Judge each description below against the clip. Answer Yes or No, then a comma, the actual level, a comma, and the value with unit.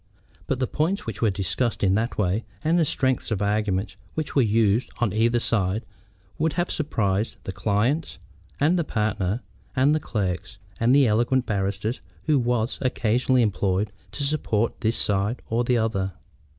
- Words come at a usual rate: Yes, average, 165 wpm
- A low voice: Yes, low, 115 Hz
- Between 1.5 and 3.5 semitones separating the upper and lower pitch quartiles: No, average, 4.3 semitones